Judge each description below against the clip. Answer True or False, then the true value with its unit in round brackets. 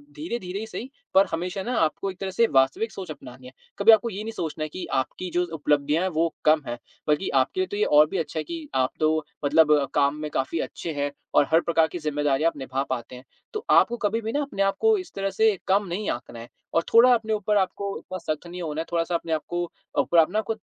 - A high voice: False (170 Hz)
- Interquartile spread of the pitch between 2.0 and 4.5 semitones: False (5.3 semitones)